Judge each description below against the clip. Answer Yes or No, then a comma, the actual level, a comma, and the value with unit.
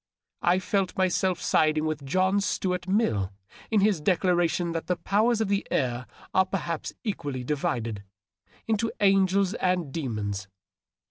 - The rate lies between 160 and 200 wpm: No, average, 140 wpm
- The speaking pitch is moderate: Yes, medium, 180 Hz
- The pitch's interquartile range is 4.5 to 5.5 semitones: Yes, average, 5.1 semitones